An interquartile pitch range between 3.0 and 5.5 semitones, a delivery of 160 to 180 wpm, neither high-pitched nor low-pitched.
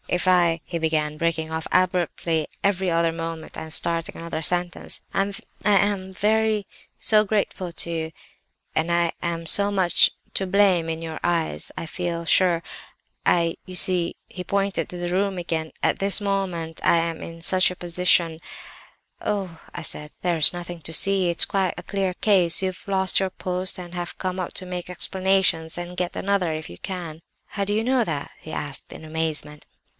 No: narrow, 2.4 semitones; average, 175 wpm; medium, 175 Hz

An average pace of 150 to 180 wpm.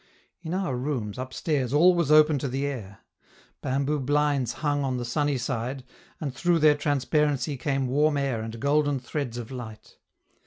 Yes: average, 165 wpm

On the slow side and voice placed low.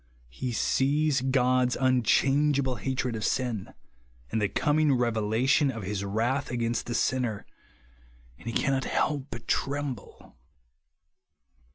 Yes: slow, 110 wpm; low, 125 Hz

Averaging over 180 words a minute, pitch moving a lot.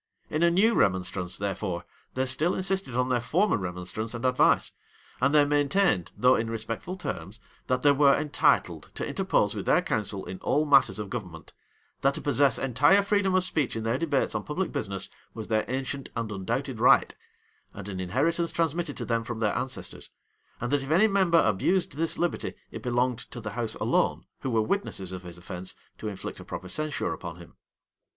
Yes: average, 190 wpm; wide, 6.3 semitones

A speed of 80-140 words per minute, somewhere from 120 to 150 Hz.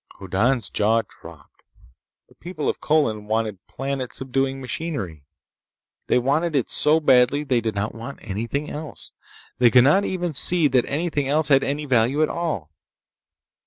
No: average, 160 wpm; low, 135 Hz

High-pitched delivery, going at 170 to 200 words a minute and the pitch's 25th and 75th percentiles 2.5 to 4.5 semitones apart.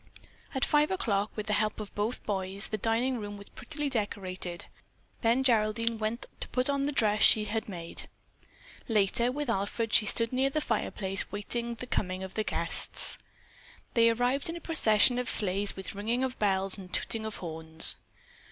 Yes: high, 220 Hz; average, 180 wpm; average, 3.6 semitones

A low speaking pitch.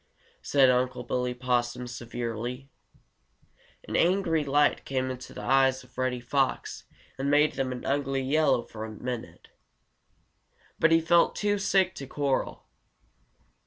Yes: low, 130 Hz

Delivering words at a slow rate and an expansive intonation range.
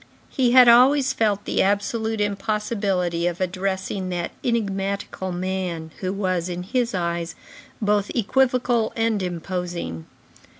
No: slow, 120 wpm; average, 3.9 semitones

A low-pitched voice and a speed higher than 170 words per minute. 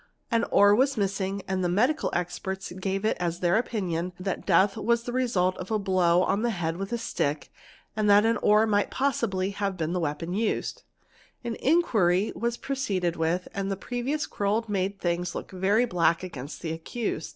No: high, 195 Hz; average, 185 wpm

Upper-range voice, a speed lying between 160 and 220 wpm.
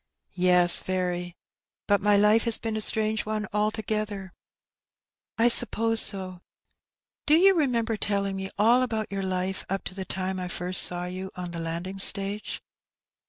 Yes: high, 200 Hz; average, 165 wpm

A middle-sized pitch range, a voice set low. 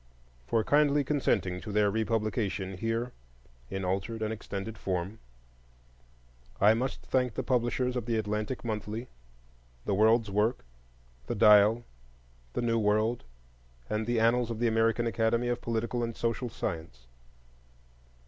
No: narrow, 2.3 semitones; low, 110 Hz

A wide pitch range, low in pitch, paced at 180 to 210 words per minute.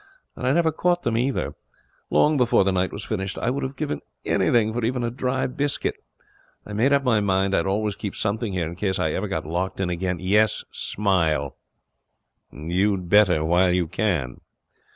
No: average, 4.8 semitones; low, 100 Hz; average, 190 wpm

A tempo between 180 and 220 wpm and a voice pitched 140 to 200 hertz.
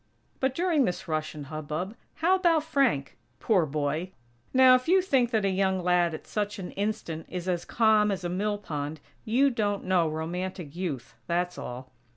Yes: average, 185 wpm; medium, 185 Hz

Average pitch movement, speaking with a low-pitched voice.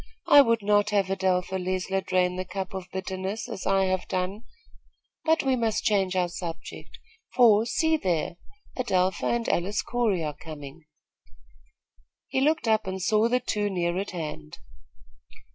No: average, 3.3 semitones; high, 190 Hz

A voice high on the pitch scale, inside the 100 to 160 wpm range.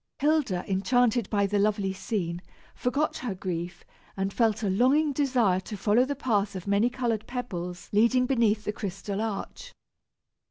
Yes: high, 215 Hz; average, 155 wpm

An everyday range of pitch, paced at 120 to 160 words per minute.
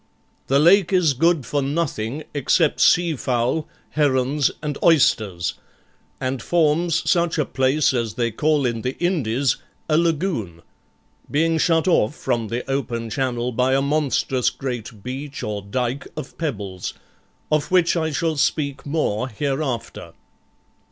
Yes: average, 4.6 semitones; average, 140 wpm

